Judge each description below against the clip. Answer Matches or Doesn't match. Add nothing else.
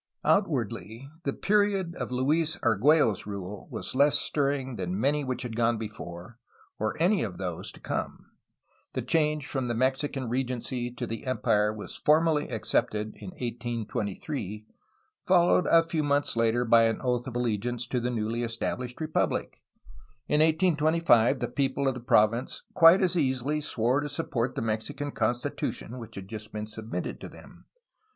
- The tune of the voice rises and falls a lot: Doesn't match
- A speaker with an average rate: Matches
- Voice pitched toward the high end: Doesn't match